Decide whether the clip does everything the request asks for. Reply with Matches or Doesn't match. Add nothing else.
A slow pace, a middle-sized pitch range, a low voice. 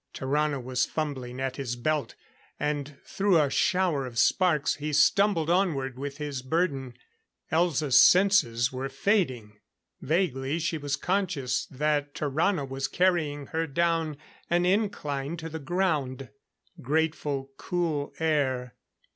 Doesn't match